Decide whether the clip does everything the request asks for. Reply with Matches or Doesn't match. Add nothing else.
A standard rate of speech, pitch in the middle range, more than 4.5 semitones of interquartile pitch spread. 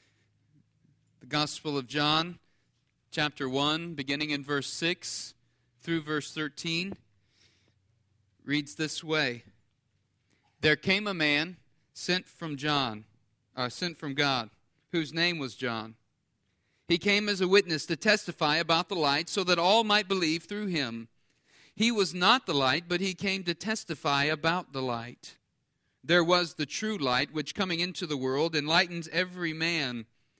Matches